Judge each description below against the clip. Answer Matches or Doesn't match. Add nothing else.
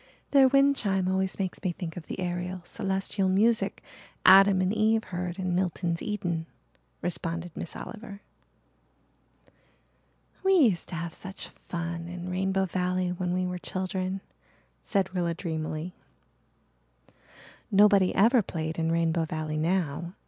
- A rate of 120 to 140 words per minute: Matches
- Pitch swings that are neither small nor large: Doesn't match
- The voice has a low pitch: Doesn't match